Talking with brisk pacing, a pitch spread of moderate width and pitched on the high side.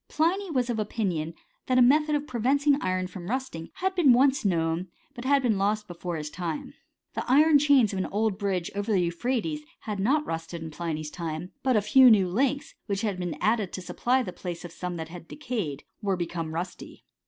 No: fast, 210 wpm; wide, 7.1 semitones; high, 205 Hz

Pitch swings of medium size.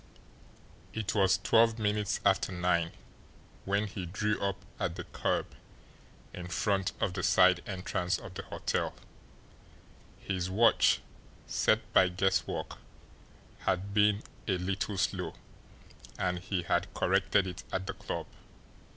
No: narrow, 2.1 semitones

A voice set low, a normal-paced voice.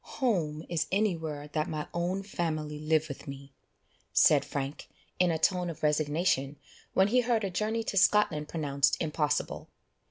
No: medium, 160 Hz; average, 155 wpm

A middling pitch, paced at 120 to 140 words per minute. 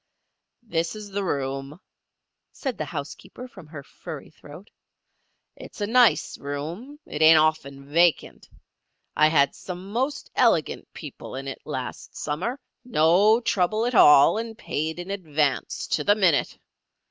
Yes: medium, 170 Hz; slow, 135 wpm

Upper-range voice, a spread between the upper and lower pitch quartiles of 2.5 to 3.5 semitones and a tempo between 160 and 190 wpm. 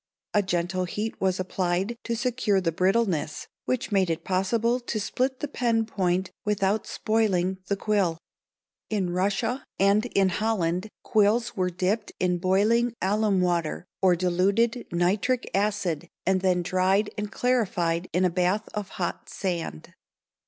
No: high, 195 Hz; average, 3.2 semitones; average, 145 wpm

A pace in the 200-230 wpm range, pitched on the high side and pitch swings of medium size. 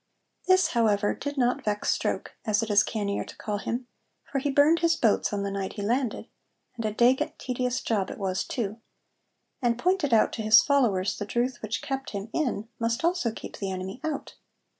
Yes: fast, 205 wpm; high, 230 Hz; average, 4.6 semitones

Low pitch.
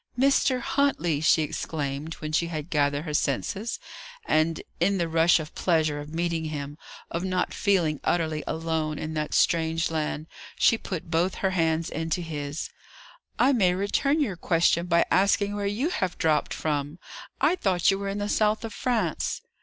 No: medium, 165 Hz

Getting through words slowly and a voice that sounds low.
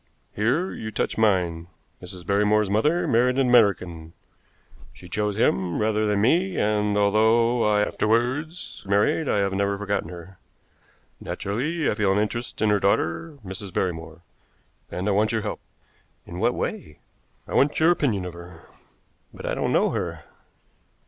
No: average, 155 wpm; low, 105 Hz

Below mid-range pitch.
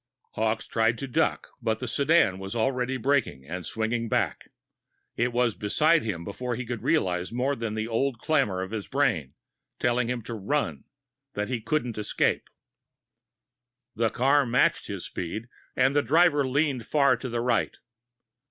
Yes: low, 120 Hz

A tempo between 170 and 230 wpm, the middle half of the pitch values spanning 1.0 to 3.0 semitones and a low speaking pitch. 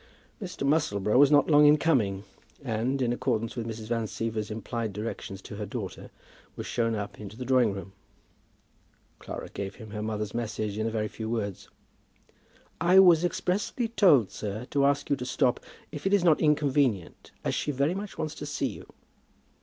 No: average, 185 wpm; wide, 5.4 semitones; low, 120 Hz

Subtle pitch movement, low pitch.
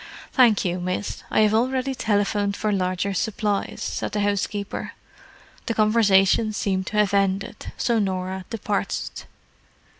No: narrow, 2.0 semitones; high, 205 Hz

